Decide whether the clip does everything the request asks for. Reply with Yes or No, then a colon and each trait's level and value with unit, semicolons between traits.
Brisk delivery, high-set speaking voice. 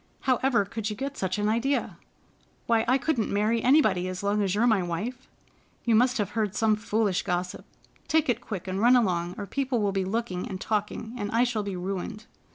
Yes: fast, 215 wpm; high, 215 Hz